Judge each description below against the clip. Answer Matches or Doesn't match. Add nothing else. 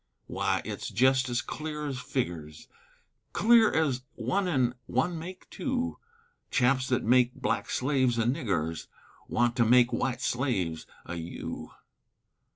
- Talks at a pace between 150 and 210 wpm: Doesn't match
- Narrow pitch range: Doesn't match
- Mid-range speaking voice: Doesn't match